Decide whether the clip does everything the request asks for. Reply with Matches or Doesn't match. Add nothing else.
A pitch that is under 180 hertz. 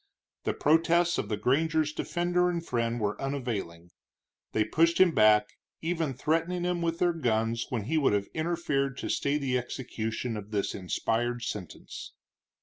Matches